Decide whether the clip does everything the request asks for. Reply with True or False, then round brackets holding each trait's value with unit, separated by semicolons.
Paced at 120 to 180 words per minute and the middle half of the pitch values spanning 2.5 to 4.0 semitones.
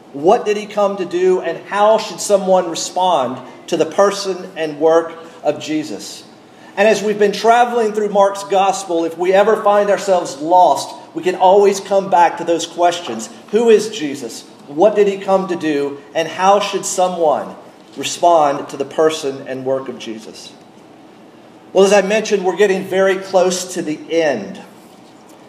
True (170 wpm; 3.7 semitones)